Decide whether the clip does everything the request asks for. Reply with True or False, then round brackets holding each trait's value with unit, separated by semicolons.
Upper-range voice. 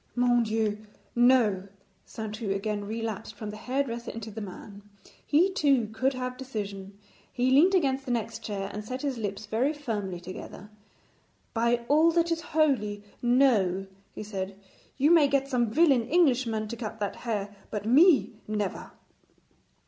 True (230 Hz)